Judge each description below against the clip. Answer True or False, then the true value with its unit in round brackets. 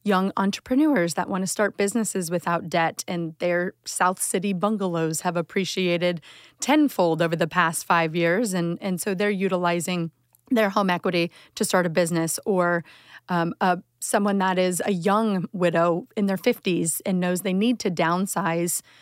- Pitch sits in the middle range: True (180 Hz)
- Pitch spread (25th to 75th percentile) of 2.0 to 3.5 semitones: True (2.9 semitones)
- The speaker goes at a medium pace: True (165 wpm)